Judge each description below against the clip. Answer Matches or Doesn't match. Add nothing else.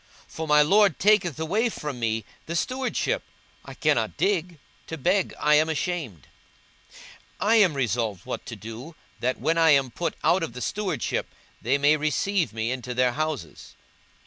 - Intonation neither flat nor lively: Doesn't match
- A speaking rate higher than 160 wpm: Matches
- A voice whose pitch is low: Doesn't match